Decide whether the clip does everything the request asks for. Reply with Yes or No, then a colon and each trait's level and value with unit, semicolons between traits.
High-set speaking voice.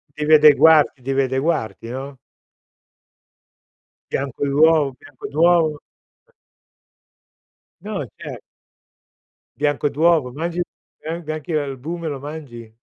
No: medium, 150 Hz